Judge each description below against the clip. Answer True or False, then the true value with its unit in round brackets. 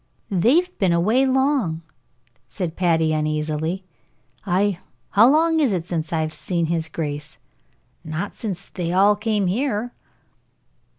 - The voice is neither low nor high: True (180 Hz)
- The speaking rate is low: True (125 wpm)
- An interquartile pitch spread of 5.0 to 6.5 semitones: True (5.4 semitones)